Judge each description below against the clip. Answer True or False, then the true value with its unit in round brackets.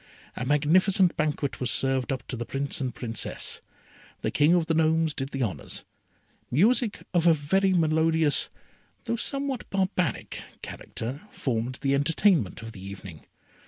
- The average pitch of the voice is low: False (150 Hz)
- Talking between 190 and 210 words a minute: False (150 wpm)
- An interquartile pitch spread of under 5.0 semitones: False (5.4 semitones)